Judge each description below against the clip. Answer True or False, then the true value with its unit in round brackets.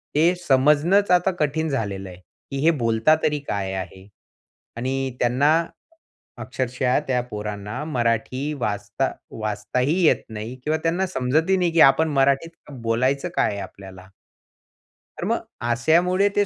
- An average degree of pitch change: False (6.1 semitones)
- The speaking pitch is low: True (130 Hz)